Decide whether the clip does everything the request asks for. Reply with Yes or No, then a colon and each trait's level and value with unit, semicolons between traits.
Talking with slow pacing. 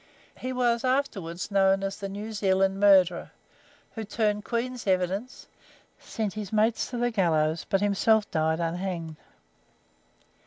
Yes: slow, 130 wpm